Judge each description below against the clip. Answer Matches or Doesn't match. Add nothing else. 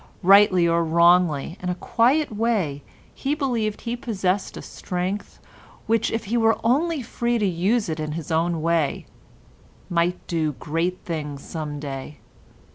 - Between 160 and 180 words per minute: Doesn't match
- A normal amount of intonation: Doesn't match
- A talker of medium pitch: Matches